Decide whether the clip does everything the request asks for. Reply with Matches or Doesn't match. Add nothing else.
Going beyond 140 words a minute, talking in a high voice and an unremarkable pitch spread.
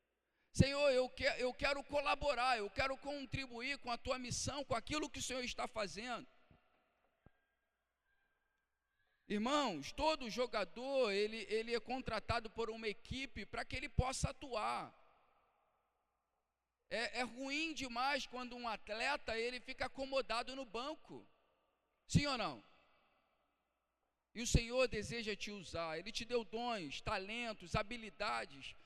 Doesn't match